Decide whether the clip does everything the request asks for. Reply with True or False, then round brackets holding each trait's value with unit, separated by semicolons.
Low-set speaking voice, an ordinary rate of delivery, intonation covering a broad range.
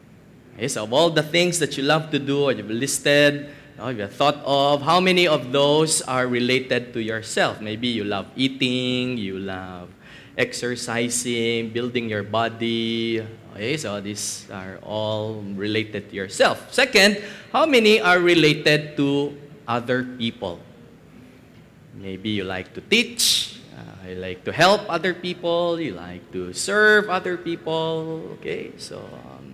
True (125 Hz; 145 wpm; 6.4 semitones)